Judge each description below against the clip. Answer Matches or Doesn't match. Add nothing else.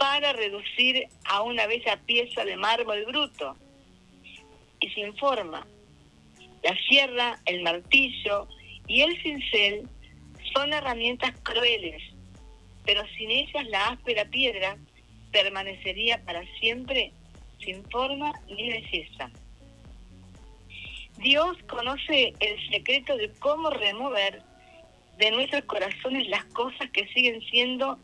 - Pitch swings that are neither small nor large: Doesn't match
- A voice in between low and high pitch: Doesn't match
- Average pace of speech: Doesn't match